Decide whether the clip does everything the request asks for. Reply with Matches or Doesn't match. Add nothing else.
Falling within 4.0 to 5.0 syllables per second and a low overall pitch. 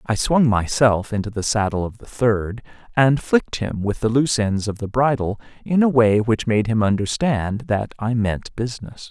Matches